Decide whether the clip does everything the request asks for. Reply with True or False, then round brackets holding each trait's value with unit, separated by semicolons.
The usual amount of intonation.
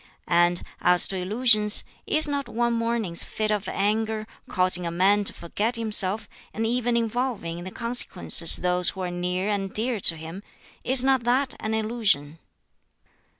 True (4.5 semitones)